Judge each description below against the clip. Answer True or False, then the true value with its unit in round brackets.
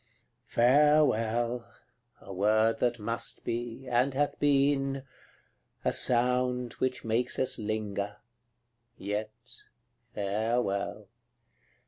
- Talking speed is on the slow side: True (90 wpm)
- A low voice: True (120 Hz)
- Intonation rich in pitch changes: False (2.8 semitones)